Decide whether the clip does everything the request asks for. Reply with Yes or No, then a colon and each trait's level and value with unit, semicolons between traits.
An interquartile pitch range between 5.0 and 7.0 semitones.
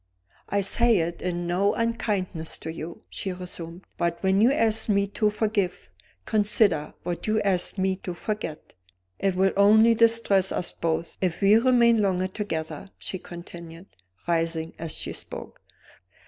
No: average, 3.6 semitones